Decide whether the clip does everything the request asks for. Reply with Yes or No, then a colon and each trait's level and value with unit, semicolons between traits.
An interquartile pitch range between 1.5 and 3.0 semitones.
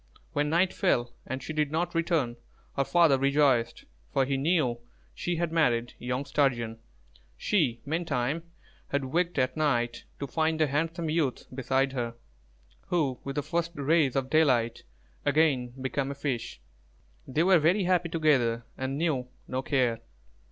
No: average, 4.1 semitones